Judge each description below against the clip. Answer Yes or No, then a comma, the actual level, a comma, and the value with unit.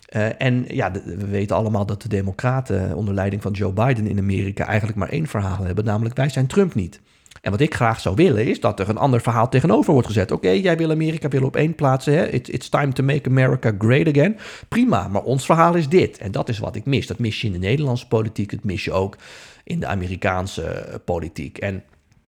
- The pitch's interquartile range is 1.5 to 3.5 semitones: No, average, 5.2 semitones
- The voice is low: Yes, low, 115 Hz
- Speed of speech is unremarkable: No, fast, 230 wpm